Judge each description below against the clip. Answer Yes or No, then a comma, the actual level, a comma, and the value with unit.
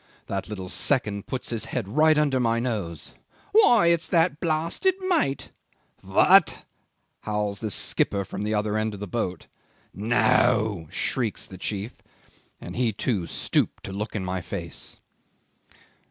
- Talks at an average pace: Yes, average, 145 wpm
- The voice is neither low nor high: No, low, 110 Hz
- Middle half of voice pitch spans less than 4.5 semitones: No, wide, 5.5 semitones